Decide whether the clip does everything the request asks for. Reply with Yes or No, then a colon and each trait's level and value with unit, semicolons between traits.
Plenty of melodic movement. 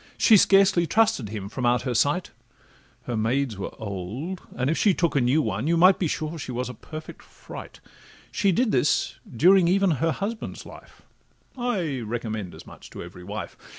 Yes: wide, 7.9 semitones